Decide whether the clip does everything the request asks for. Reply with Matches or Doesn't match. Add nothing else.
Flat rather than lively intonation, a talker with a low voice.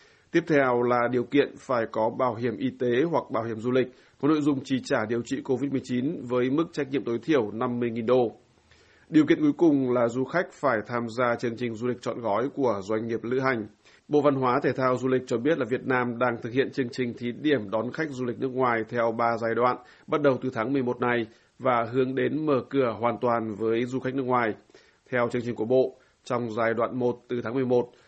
Matches